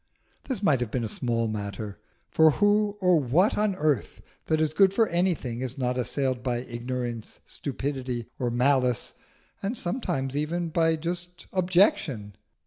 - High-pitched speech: No, medium, 140 Hz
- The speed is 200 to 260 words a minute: No, average, 150 wpm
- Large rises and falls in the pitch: Yes, wide, 6.4 semitones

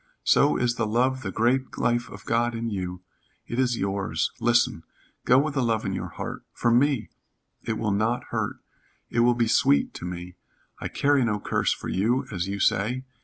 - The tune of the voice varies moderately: Yes, average, 3.6 semitones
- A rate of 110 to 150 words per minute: No, average, 195 wpm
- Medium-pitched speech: No, low, 115 Hz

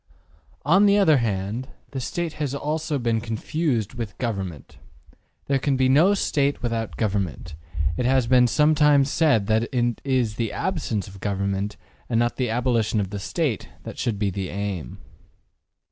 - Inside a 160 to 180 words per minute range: Yes, average, 165 wpm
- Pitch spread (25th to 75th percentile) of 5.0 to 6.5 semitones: Yes, wide, 5.5 semitones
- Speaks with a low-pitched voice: Yes, low, 120 Hz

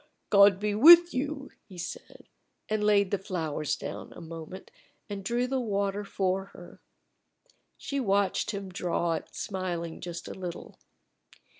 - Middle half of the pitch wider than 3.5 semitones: No, average, 3.0 semitones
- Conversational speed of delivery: Yes, average, 145 wpm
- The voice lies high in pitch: Yes, high, 195 Hz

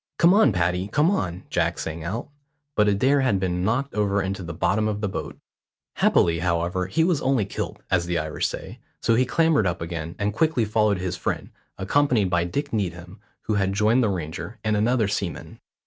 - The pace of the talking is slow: No, average, 195 wpm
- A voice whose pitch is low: Yes, low, 100 Hz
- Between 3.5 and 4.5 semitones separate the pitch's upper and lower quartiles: No, average, 4.9 semitones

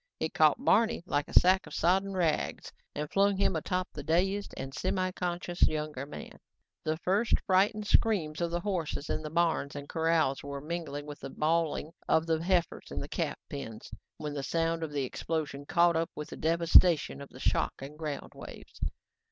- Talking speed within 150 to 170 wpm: No, average, 185 wpm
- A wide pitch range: No, average, 3.3 semitones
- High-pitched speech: No, medium, 165 Hz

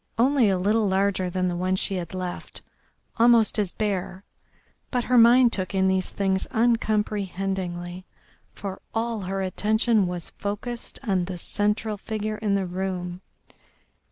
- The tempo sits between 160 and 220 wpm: No, average, 145 wpm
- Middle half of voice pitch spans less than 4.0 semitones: Yes, average, 2.8 semitones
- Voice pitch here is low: No, high, 195 Hz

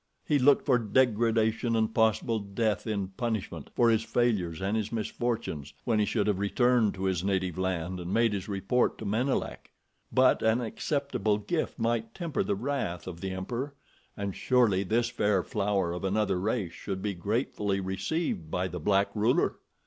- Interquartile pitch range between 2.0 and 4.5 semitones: Yes, average, 3.7 semitones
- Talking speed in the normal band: Yes, average, 170 wpm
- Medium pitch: No, low, 105 Hz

